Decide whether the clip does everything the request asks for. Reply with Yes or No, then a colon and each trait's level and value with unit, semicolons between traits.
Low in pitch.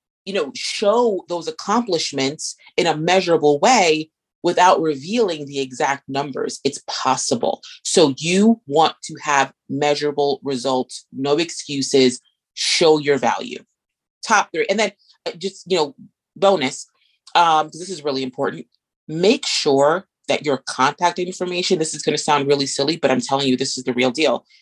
No: medium, 155 Hz